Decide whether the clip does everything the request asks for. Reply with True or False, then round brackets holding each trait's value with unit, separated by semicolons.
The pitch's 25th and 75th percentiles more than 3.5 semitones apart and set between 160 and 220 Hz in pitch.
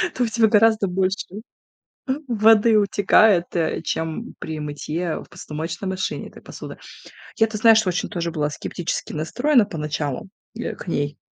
True (5.3 semitones; 185 Hz)